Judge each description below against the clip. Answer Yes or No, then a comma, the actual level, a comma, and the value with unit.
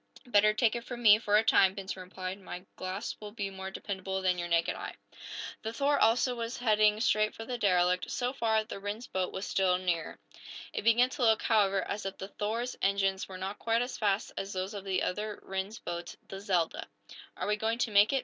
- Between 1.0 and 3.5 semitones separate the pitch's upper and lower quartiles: Yes, average, 2.8 semitones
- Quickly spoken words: Yes, fast, 220 wpm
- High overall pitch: Yes, high, 205 Hz